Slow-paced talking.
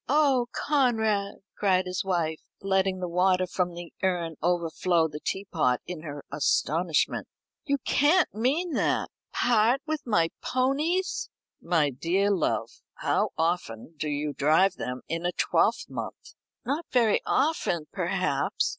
Yes: slow, 130 wpm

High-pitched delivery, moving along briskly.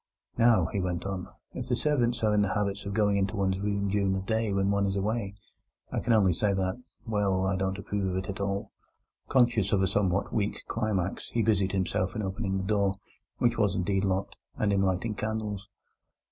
No: low, 100 Hz; fast, 210 wpm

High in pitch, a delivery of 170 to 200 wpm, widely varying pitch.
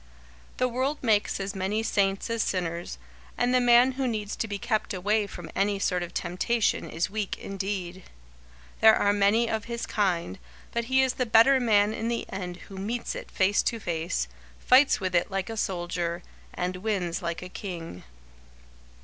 No: high, 205 Hz; average, 180 wpm; average, 4.0 semitones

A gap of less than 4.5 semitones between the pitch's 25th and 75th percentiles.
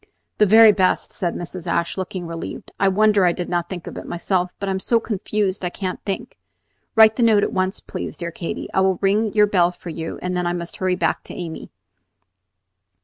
Yes: average, 2.8 semitones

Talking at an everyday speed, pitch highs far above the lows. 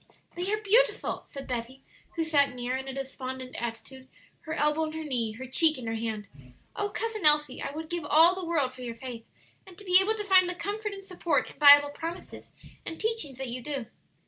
No: fast, 225 wpm; wide, 5.7 semitones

